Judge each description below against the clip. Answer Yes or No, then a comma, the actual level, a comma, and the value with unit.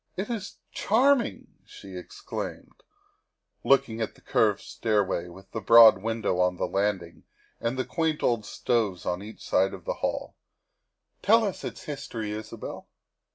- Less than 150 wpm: No, average, 155 wpm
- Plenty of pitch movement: Yes, wide, 6.1 semitones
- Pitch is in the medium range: No, low, 110 Hz